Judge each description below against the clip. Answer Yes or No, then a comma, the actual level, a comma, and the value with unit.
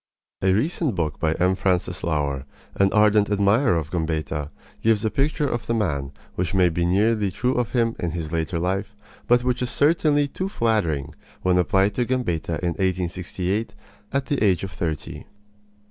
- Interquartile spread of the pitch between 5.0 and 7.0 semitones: Yes, wide, 5.4 semitones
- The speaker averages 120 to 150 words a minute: No, average, 175 wpm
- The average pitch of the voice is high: No, very low, 95 Hz